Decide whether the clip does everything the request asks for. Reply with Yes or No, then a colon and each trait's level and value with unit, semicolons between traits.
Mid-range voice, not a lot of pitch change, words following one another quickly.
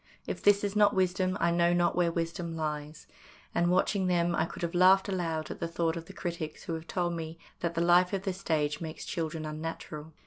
Yes: medium, 170 Hz; narrow, 2.0 semitones; fast, 220 wpm